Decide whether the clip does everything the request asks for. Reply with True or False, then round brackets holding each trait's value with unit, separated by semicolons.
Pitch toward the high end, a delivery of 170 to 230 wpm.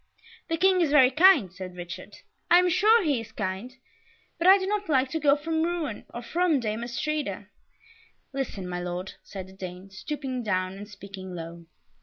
True (250 Hz; 185 wpm)